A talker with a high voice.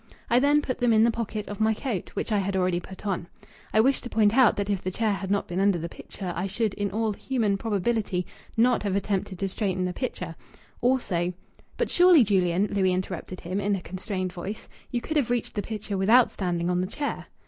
Yes: high, 200 Hz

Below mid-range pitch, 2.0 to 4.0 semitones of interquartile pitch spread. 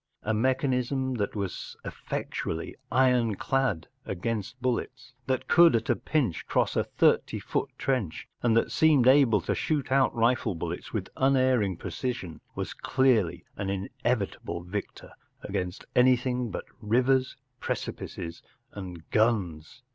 No: low, 120 Hz; average, 4.7 semitones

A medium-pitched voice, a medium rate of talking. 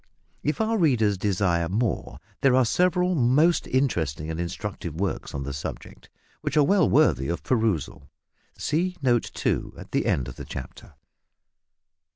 No: low, 115 Hz; average, 155 wpm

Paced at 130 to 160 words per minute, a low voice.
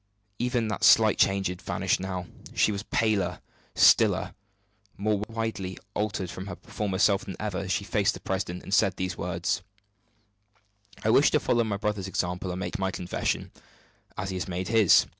No: average, 180 wpm; low, 100 Hz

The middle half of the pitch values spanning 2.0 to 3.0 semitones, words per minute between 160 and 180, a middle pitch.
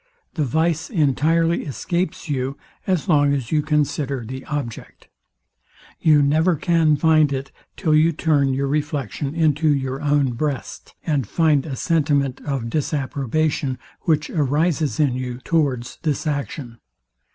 No: narrow, 2.6 semitones; slow, 135 wpm; medium, 145 Hz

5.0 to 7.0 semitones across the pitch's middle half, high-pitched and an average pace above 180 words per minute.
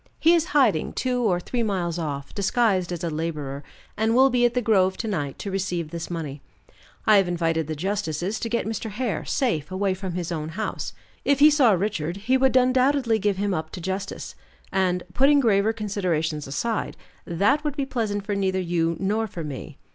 Yes: wide, 5.4 semitones; high, 195 Hz; average, 200 wpm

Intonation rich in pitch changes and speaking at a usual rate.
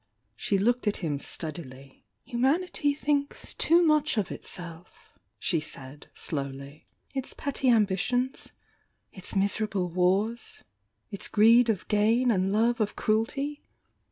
No: wide, 5.8 semitones; slow, 130 wpm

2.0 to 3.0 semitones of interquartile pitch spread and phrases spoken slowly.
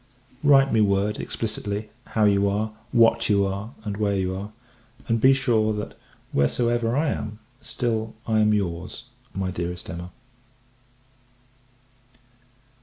Yes: narrow, 2.6 semitones; slow, 130 wpm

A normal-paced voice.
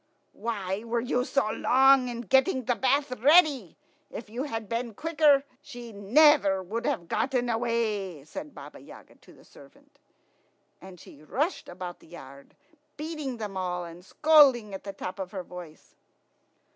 Yes: average, 160 wpm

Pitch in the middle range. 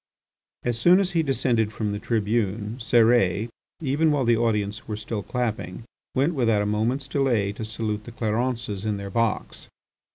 No: low, 115 Hz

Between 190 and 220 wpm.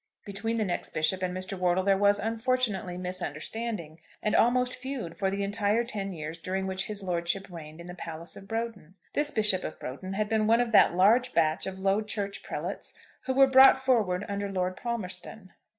Yes: average, 195 wpm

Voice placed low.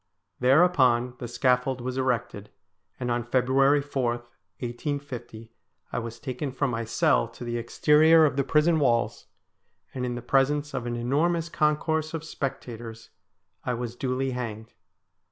Yes: low, 125 Hz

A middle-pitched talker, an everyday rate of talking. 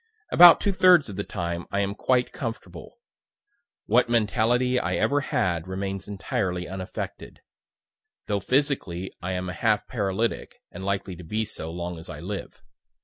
No: low, 100 Hz; average, 155 wpm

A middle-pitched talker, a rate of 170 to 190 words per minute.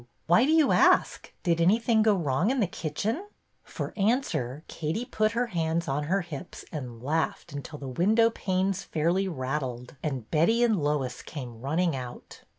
Yes: medium, 165 Hz; average, 175 wpm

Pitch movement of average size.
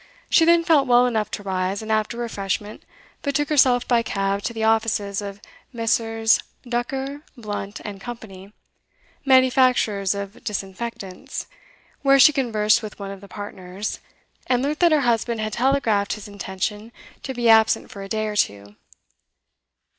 Yes: average, 3.6 semitones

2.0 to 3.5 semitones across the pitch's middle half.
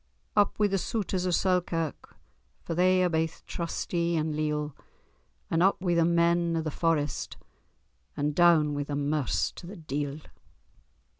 Yes: average, 2.8 semitones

